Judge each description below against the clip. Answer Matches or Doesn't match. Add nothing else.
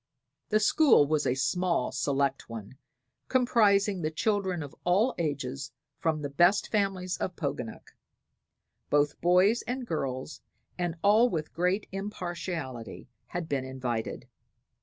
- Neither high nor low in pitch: Matches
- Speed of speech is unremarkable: Doesn't match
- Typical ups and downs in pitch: Doesn't match